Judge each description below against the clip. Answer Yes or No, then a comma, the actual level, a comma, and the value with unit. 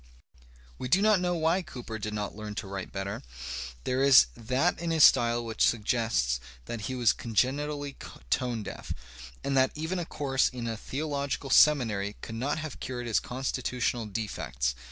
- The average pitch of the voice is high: No, low, 125 Hz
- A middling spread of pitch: Yes, average, 4.9 semitones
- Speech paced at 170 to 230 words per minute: Yes, average, 175 wpm